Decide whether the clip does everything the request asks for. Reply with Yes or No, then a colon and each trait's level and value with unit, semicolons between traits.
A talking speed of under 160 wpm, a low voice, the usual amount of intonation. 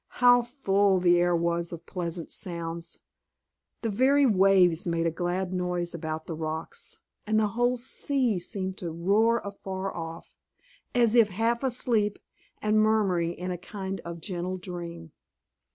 No: average, 150 wpm; medium, 185 Hz; average, 4.1 semitones